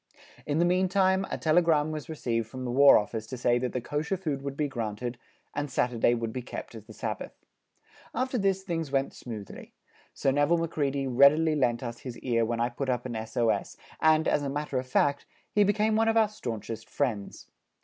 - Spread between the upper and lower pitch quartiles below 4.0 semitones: No, average, 5.2 semitones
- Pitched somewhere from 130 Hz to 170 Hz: Yes, medium, 140 Hz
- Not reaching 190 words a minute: No, average, 200 wpm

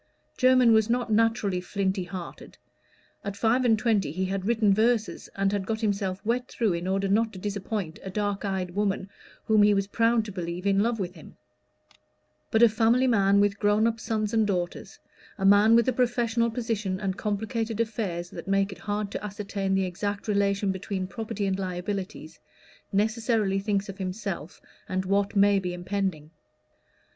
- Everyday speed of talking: Yes, average, 175 wpm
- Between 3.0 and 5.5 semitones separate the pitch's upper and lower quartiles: No, narrow, 2.5 semitones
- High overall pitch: Yes, high, 200 Hz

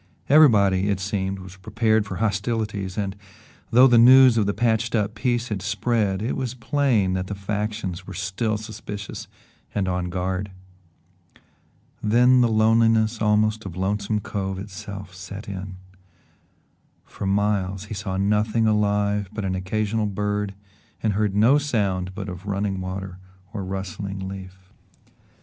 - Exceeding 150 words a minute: No, average, 145 wpm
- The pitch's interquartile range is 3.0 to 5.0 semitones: No, narrow, 2.4 semitones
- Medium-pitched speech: No, low, 105 Hz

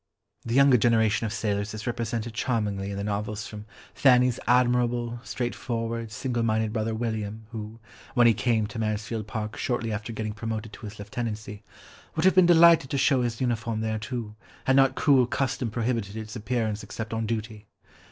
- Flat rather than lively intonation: Yes, narrow, 2.2 semitones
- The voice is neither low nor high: No, low, 115 Hz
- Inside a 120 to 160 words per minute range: No, average, 175 wpm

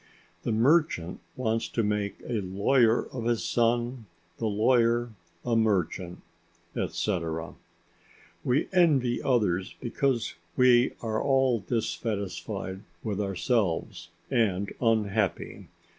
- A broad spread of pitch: No, average, 3.4 semitones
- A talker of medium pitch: No, low, 115 Hz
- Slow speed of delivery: Yes, slow, 100 wpm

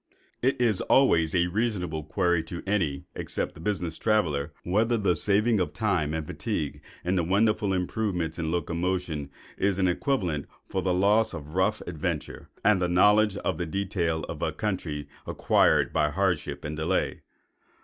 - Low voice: Yes, very low, 90 Hz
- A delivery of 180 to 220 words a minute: No, average, 160 wpm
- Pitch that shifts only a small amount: No, average, 4.2 semitones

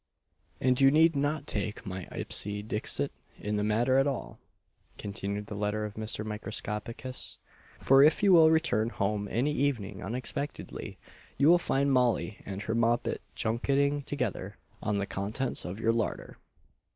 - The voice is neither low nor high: No, low, 115 Hz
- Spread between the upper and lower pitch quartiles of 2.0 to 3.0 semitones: No, average, 5.0 semitones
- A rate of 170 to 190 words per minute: No, average, 150 wpm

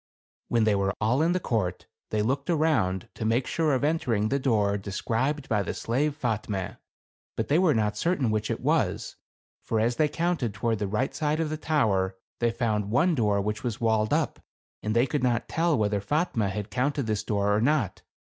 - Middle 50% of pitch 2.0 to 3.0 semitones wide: No, wide, 5.6 semitones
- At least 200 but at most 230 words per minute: Yes, fast, 205 wpm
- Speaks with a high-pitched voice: No, low, 115 Hz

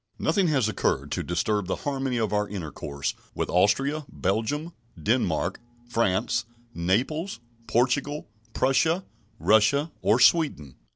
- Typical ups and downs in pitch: No, wide, 6.4 semitones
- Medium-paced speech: No, slow, 115 wpm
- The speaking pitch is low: Yes, low, 120 Hz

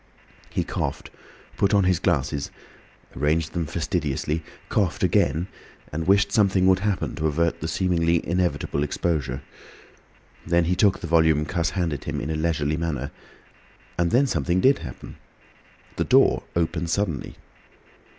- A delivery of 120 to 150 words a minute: Yes, average, 140 wpm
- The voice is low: Yes, very low, 85 Hz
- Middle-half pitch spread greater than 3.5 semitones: No, average, 3.1 semitones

